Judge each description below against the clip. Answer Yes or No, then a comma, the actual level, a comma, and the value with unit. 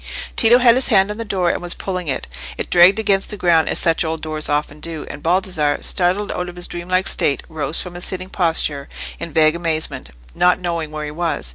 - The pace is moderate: No, fast, 225 wpm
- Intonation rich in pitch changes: No, average, 3.1 semitones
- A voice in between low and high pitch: Yes, medium, 175 Hz